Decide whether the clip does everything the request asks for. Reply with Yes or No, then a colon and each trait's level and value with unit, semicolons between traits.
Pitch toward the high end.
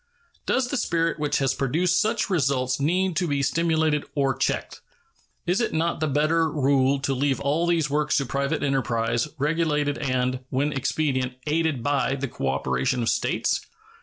No: medium, 145 Hz